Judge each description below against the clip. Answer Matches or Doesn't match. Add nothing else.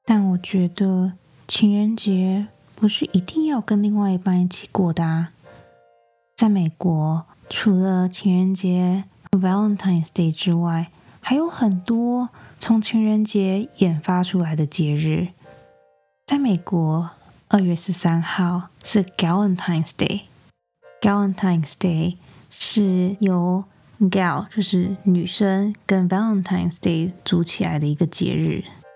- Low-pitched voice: Doesn't match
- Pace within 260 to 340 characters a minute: Matches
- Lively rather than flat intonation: Doesn't match